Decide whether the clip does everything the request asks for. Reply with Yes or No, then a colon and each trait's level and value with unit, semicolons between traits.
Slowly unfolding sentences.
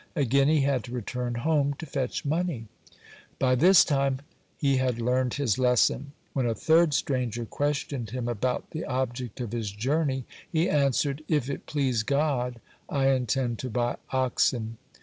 No: average, 155 wpm